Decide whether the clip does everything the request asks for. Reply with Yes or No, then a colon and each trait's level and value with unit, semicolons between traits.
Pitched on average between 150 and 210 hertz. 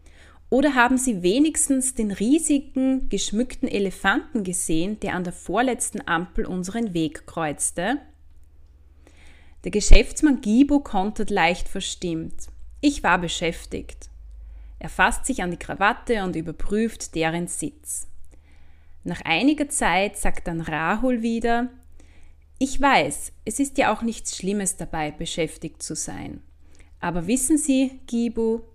Yes: high, 190 Hz